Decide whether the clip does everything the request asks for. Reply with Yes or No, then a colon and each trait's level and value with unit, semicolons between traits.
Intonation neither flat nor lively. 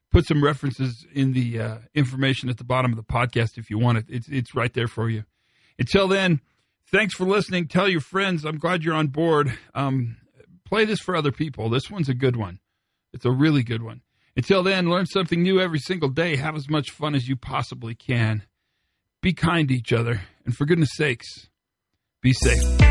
No: wide, 5.8 semitones